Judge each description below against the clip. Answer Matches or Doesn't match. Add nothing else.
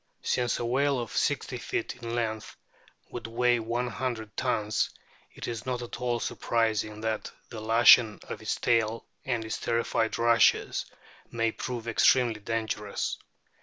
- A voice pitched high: Doesn't match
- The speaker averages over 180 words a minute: Doesn't match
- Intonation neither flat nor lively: Doesn't match